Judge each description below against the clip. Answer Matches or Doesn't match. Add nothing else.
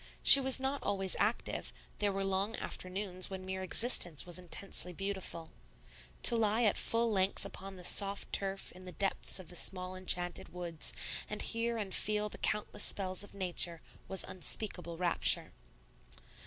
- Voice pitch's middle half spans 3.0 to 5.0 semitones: Doesn't match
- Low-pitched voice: Doesn't match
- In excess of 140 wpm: Matches